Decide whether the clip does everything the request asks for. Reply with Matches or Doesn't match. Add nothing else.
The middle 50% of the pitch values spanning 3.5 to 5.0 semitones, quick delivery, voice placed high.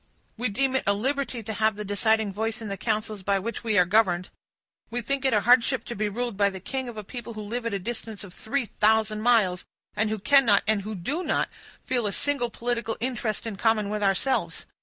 Doesn't match